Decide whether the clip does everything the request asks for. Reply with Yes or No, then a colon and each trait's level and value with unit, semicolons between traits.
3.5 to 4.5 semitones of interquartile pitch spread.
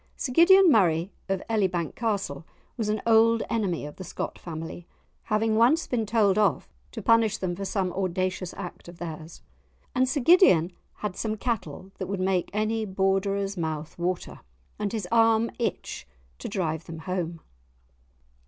Yes: average, 4.2 semitones